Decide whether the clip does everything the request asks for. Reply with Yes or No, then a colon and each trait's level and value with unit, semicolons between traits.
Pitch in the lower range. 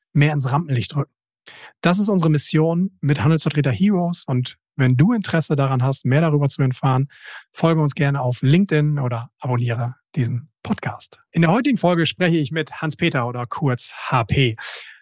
No: medium, 145 Hz